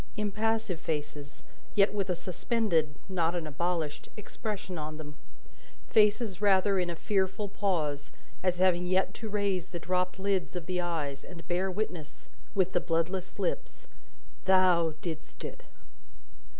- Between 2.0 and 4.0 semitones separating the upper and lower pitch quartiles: Yes, average, 3.0 semitones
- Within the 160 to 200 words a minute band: No, average, 140 wpm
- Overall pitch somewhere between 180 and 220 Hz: Yes, medium, 185 Hz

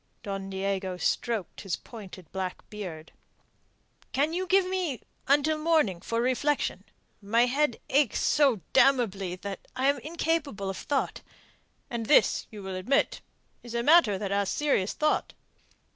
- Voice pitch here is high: Yes, high, 235 Hz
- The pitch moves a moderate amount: No, wide, 7.1 semitones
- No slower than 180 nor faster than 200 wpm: No, average, 145 wpm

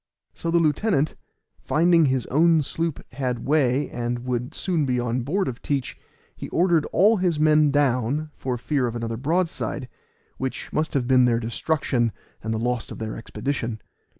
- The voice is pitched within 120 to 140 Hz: Yes, low, 135 Hz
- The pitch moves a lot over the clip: No, average, 4.4 semitones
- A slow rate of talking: No, average, 170 wpm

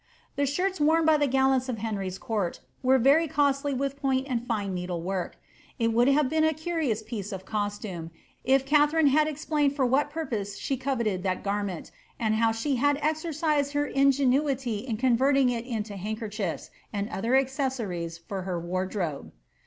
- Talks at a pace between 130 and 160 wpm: No, average, 175 wpm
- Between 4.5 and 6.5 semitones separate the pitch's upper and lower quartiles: Yes, wide, 5.6 semitones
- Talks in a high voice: Yes, very high, 255 Hz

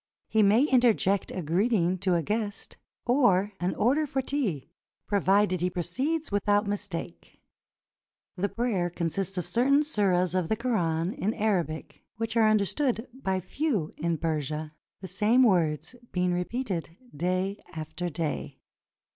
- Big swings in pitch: No, average, 4.6 semitones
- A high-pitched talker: Yes, high, 195 Hz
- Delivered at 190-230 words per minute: No, average, 145 wpm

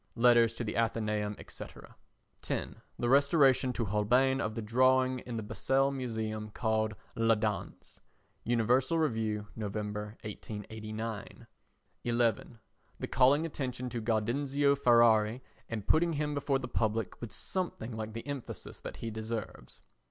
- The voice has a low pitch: Yes, low, 115 Hz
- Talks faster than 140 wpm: No, slow, 135 wpm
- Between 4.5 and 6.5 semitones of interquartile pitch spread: No, average, 3.2 semitones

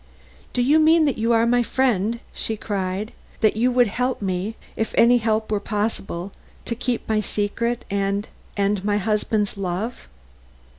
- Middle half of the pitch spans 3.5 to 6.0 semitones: No, average, 2.9 semitones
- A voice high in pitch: Yes, high, 220 Hz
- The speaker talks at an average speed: Yes, average, 155 wpm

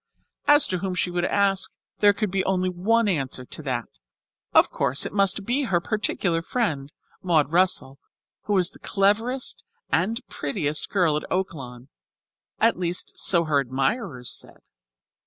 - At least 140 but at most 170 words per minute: Yes, average, 155 wpm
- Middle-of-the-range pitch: Yes, medium, 180 Hz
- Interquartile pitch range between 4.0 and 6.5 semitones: Yes, average, 5.3 semitones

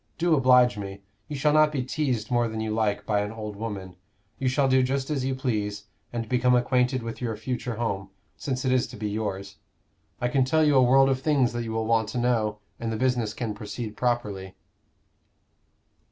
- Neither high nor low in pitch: No, low, 120 Hz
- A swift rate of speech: Yes, fast, 210 wpm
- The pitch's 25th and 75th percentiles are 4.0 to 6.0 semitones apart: No, average, 3.4 semitones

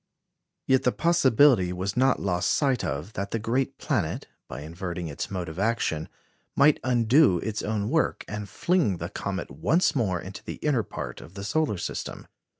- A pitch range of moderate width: No, wide, 6.7 semitones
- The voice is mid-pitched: No, low, 105 Hz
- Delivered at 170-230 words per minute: Yes, average, 175 wpm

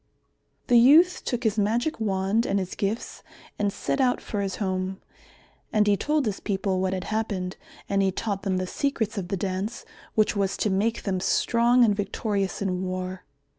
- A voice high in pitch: Yes, high, 200 Hz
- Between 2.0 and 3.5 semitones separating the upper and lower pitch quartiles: Yes, average, 3.1 semitones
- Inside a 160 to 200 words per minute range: Yes, average, 185 wpm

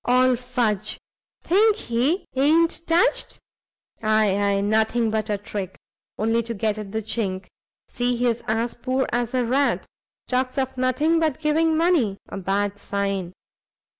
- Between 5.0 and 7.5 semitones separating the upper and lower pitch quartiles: No, average, 3.9 semitones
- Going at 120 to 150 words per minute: Yes, average, 145 wpm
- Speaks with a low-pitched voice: No, high, 235 Hz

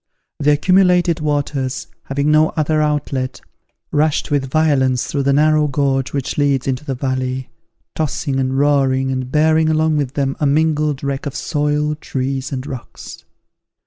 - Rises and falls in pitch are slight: Yes, narrow, 2.3 semitones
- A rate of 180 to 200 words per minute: No, average, 150 wpm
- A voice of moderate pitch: Yes, medium, 145 Hz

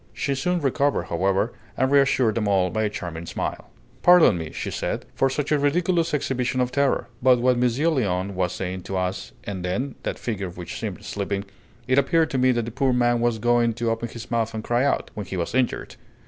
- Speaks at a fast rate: Yes, fast, 220 wpm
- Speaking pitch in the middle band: No, low, 120 Hz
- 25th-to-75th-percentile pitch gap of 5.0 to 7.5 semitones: Yes, average, 5.3 semitones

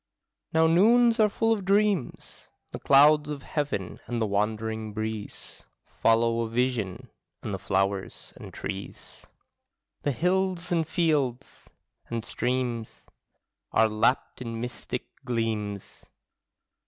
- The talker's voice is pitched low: Yes, low, 120 Hz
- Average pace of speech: No, slow, 115 wpm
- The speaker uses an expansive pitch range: Yes, wide, 6.7 semitones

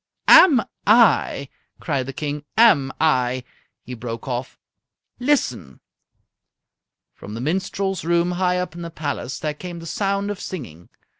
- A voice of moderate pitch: Yes, medium, 160 Hz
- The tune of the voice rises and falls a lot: Yes, wide, 6.6 semitones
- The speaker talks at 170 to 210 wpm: No, average, 140 wpm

